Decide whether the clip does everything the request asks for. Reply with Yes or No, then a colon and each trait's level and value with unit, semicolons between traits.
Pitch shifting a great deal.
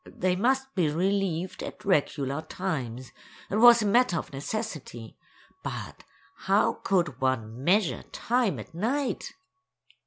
Yes: wide, 7.6 semitones